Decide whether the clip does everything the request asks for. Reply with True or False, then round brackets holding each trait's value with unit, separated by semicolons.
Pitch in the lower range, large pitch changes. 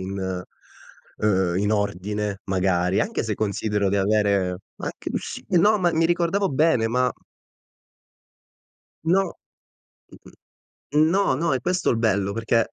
True (110 Hz; 8.8 semitones)